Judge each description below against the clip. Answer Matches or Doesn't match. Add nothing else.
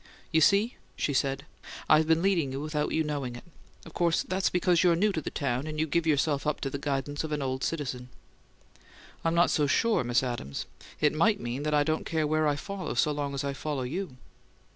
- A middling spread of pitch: Matches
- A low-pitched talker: Doesn't match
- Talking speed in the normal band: Doesn't match